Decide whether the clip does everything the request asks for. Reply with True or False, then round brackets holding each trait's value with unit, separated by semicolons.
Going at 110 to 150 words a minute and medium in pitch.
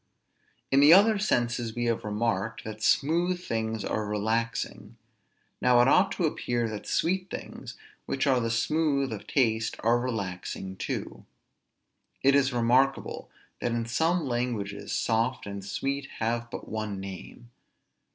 False (140 wpm; 120 Hz)